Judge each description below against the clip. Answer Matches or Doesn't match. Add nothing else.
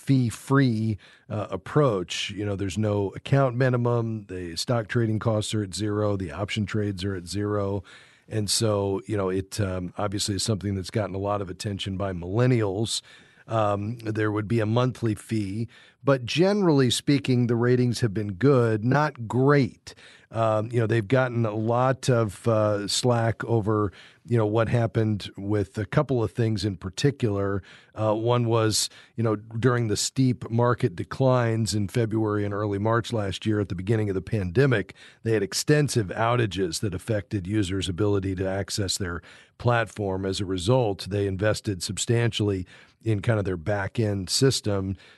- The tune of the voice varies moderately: Matches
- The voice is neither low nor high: Doesn't match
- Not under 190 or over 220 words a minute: Doesn't match